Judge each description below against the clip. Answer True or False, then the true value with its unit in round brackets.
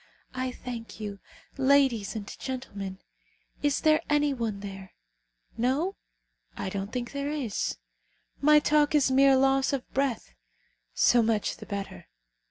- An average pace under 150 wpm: True (135 wpm)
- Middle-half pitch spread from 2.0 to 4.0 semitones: False (5.2 semitones)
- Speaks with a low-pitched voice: False (255 Hz)